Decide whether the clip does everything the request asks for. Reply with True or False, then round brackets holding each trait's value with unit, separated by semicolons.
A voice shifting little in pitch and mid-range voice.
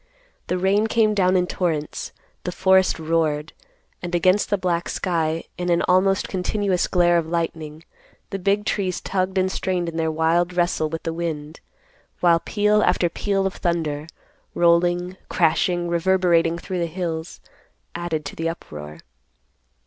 True (2.3 semitones; 175 Hz)